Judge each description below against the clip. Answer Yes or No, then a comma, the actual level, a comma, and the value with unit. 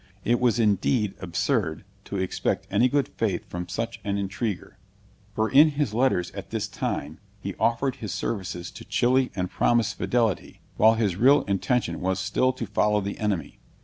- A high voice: No, low, 110 Hz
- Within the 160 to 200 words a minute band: Yes, average, 170 wpm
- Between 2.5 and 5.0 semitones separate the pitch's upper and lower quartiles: Yes, average, 4.3 semitones